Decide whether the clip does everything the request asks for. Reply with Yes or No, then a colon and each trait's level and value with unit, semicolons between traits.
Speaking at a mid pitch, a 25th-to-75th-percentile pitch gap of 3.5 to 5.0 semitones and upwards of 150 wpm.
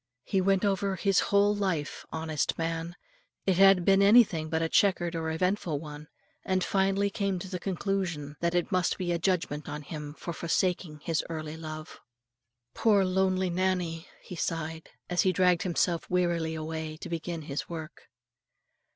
No: medium, 175 Hz; average, 3.0 semitones; average, 165 wpm